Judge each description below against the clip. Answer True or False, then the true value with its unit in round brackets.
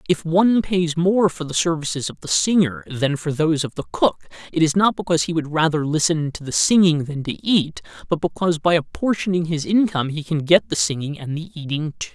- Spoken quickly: True (220 wpm)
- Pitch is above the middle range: False (155 Hz)